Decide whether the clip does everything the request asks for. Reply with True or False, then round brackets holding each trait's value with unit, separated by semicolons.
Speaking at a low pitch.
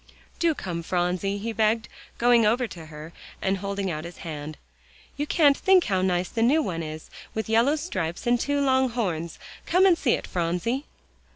False (210 Hz)